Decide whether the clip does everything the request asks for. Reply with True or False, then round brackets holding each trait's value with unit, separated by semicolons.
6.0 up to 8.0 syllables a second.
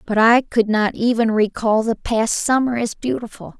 False (4.6 syllables/s)